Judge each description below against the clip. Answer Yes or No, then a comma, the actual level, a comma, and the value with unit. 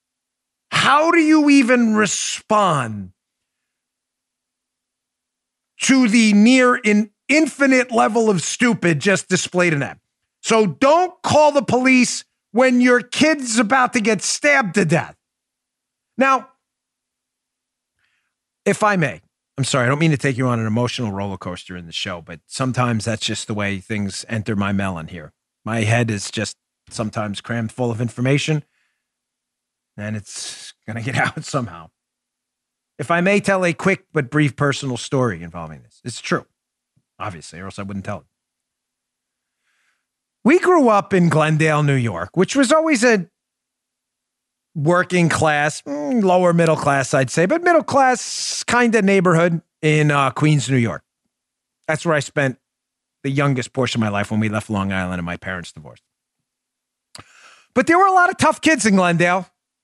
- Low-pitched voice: No, medium, 155 Hz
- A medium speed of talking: Yes, average, 160 wpm